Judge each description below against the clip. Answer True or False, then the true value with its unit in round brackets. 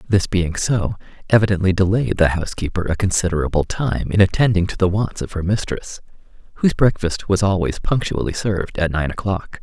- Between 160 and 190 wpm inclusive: True (170 wpm)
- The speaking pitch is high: False (95 Hz)